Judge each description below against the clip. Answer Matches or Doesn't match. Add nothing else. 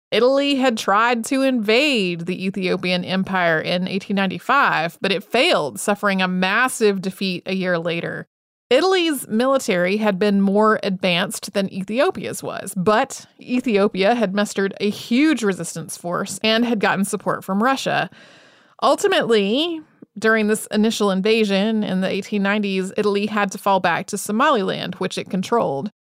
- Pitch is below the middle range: Doesn't match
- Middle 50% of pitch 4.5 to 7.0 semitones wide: Doesn't match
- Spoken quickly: Doesn't match